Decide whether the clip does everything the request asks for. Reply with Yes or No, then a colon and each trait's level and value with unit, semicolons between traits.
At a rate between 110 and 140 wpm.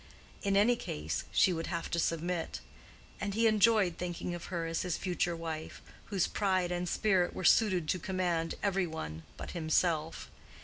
No: average, 170 wpm